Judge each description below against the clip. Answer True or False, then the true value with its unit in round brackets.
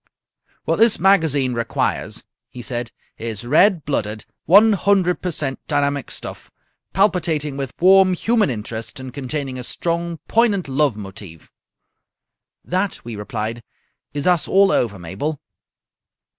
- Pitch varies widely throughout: True (7.4 semitones)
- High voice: False (145 Hz)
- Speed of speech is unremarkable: False (130 wpm)